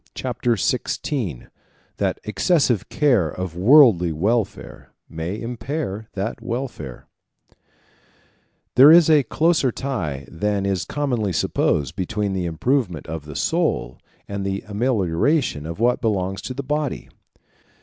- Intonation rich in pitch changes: Yes, wide, 6.5 semitones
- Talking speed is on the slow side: Yes, slow, 120 wpm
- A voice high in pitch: No, low, 105 Hz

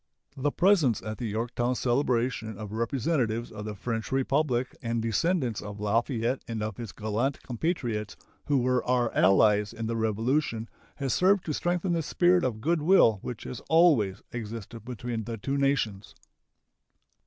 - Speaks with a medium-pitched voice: No, low, 120 Hz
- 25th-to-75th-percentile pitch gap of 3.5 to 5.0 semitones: Yes, average, 4.1 semitones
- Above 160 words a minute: No, average, 155 wpm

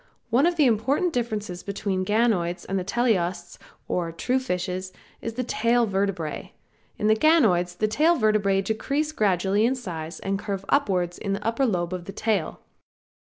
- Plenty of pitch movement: No, average, 4.5 semitones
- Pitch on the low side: No, high, 205 Hz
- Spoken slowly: No, average, 175 wpm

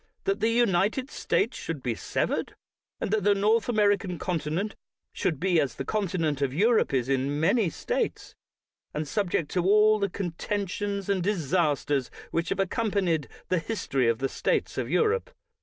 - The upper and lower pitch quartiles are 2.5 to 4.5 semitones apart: No, wide, 5.6 semitones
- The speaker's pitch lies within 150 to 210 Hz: Yes, medium, 185 Hz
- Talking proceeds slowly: No, average, 165 wpm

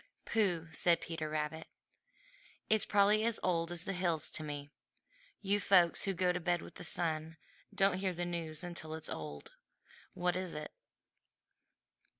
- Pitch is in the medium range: Yes, medium, 175 Hz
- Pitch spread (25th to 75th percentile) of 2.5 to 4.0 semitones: Yes, average, 2.8 semitones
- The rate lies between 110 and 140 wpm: No, average, 155 wpm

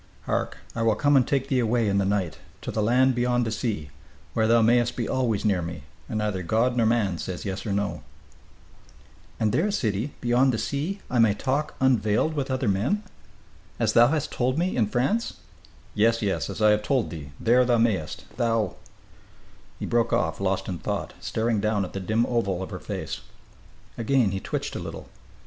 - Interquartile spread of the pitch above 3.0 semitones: Yes, average, 3.6 semitones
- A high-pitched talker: No, low, 115 Hz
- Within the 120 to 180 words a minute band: No, fast, 205 wpm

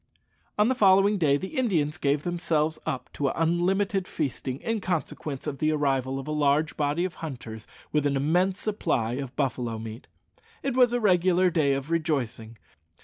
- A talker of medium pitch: Yes, medium, 155 Hz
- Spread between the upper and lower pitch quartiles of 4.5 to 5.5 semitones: Yes, average, 5.1 semitones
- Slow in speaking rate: No, average, 175 wpm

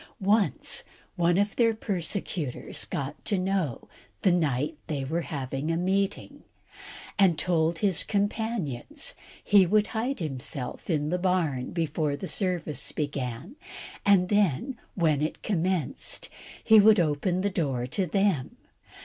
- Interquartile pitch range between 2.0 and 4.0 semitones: No, average, 5.0 semitones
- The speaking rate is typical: No, slow, 130 wpm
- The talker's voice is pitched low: No, medium, 175 Hz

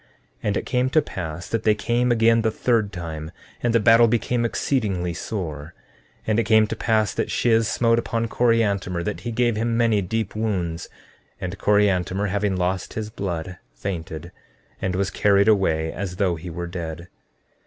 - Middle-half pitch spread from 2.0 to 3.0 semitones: No, average, 4.3 semitones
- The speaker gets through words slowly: No, average, 175 wpm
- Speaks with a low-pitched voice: Yes, low, 105 Hz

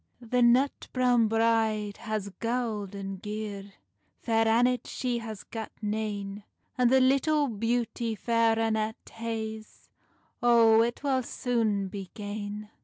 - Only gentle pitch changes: Yes, narrow, 2.2 semitones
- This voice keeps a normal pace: No, slow, 125 wpm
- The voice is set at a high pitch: Yes, high, 225 Hz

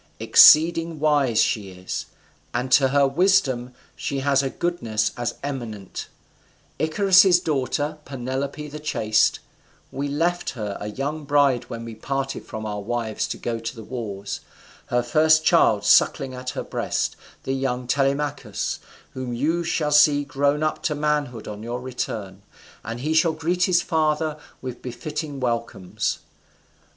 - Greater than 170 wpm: No, average, 145 wpm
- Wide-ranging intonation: No, average, 4.3 semitones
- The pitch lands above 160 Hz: No, low, 135 Hz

